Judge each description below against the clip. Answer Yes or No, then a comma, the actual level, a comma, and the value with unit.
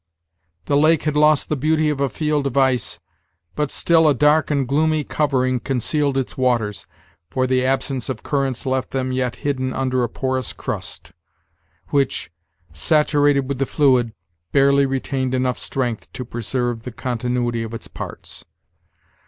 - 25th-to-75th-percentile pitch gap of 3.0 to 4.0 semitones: No, narrow, 2.4 semitones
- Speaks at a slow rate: No, average, 155 wpm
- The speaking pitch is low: Yes, low, 130 Hz